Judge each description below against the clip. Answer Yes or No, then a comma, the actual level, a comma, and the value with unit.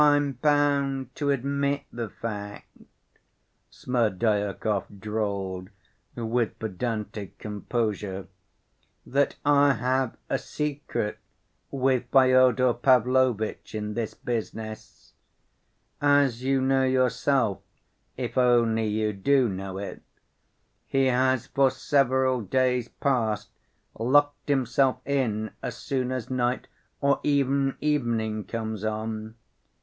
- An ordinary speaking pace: No, slow, 100 wpm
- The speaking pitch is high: No, low, 125 Hz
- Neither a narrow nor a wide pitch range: Yes, average, 3.7 semitones